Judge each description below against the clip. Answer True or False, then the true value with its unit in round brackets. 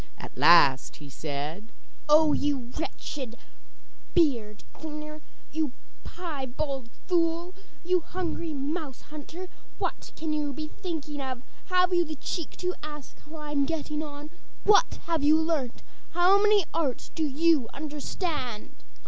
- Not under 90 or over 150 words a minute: True (135 wpm)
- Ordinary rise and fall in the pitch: True (3.4 semitones)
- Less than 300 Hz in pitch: False (305 Hz)